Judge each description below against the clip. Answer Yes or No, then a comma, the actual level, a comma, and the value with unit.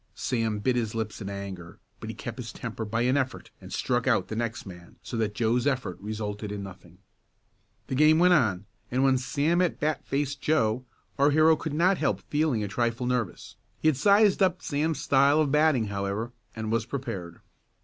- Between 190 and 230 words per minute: Yes, average, 200 wpm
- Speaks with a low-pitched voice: Yes, low, 125 Hz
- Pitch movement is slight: No, wide, 5.6 semitones